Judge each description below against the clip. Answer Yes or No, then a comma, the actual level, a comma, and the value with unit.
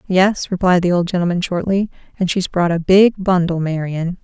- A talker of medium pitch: Yes, medium, 180 Hz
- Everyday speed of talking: Yes, average, 185 wpm